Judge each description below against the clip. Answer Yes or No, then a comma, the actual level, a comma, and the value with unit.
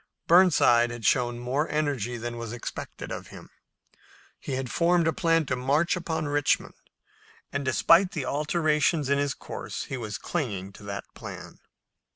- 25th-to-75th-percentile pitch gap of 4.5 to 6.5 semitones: Yes, average, 4.9 semitones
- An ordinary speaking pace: Yes, average, 160 wpm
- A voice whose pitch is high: No, medium, 140 Hz